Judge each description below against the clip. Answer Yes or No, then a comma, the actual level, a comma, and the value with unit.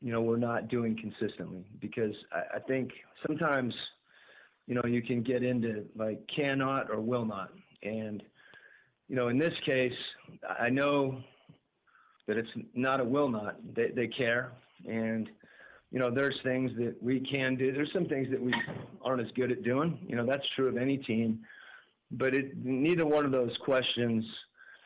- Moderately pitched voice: No, low, 125 Hz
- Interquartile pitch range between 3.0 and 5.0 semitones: No, narrow, 2.5 semitones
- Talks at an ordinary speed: Yes, average, 175 wpm